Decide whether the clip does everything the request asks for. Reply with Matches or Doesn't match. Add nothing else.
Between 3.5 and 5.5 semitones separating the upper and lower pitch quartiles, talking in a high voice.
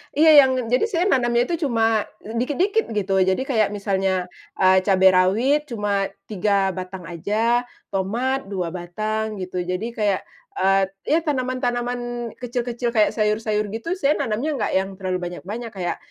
Matches